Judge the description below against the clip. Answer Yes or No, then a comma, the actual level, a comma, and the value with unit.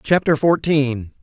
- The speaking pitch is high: No, medium, 150 Hz